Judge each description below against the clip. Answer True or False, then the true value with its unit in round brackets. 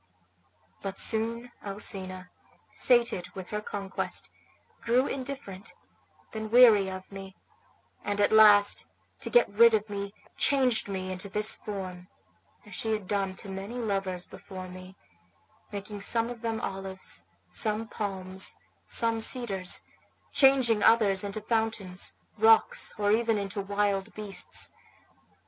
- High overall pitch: True (205 Hz)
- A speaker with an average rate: False (125 wpm)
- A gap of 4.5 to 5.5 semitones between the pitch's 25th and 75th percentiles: False (2.8 semitones)